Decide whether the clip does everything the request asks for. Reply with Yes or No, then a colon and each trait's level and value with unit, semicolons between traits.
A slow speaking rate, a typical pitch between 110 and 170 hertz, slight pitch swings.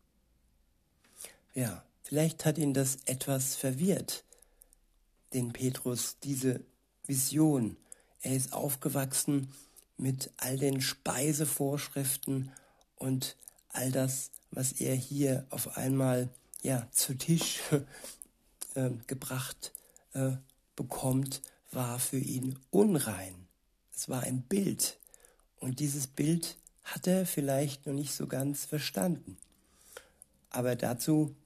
Yes: slow, 105 wpm; low, 135 Hz; narrow, 2.2 semitones